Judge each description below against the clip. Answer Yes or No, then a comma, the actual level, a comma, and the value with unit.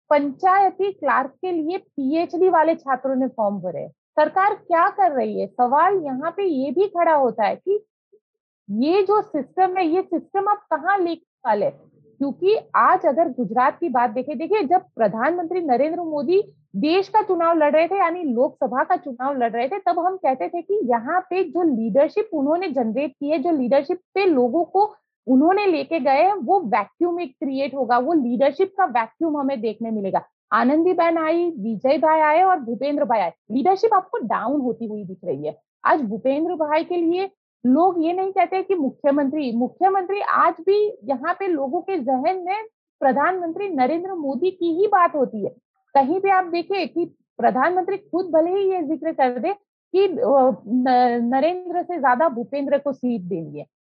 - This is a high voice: Yes, very high, 325 Hz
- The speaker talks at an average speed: Yes, average, 175 wpm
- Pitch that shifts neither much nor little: No, wide, 5.7 semitones